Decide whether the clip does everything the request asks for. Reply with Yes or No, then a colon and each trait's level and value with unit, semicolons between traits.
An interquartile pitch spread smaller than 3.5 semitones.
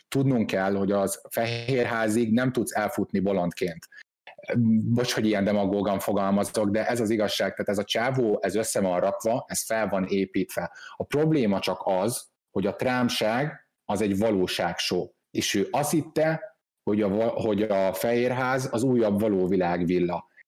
No: average, 3.9 semitones